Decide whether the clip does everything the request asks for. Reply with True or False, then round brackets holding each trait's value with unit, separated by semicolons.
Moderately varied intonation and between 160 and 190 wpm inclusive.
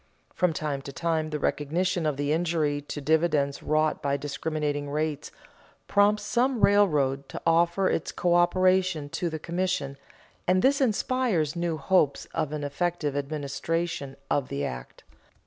False (3.8 semitones; 145 wpm)